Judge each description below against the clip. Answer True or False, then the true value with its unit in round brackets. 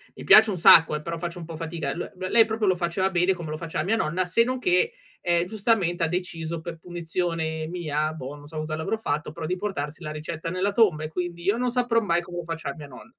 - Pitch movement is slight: False (3.0 semitones)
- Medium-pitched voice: True (170 Hz)